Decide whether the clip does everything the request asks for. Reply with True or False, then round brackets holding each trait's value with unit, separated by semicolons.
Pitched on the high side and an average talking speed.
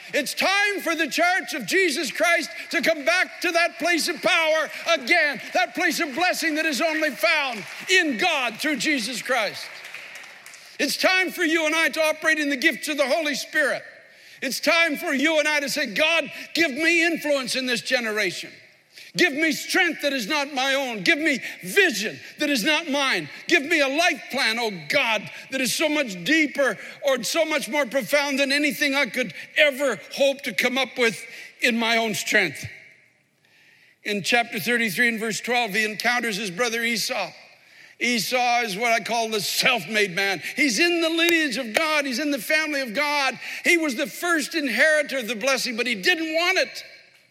True (295 Hz; 190 wpm)